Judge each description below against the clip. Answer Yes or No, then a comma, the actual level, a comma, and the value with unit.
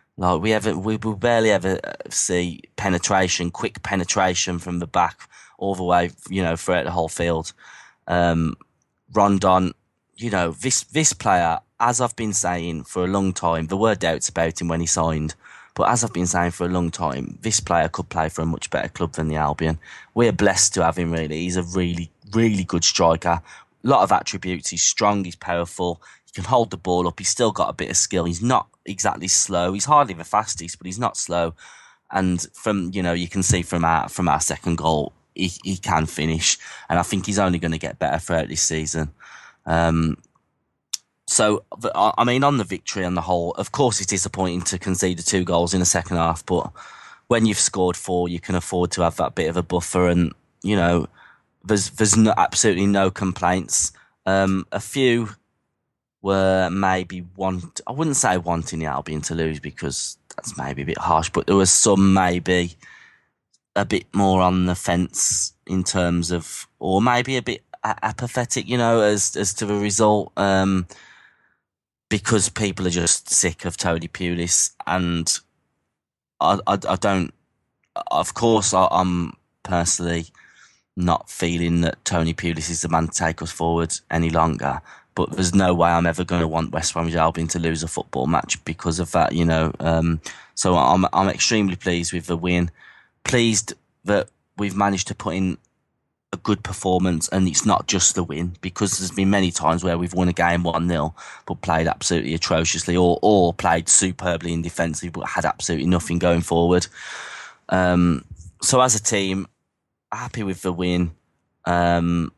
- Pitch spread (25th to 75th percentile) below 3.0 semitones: Yes, narrow, 2.6 semitones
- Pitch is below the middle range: Yes, very low, 90 Hz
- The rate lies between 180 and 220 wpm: Yes, average, 185 wpm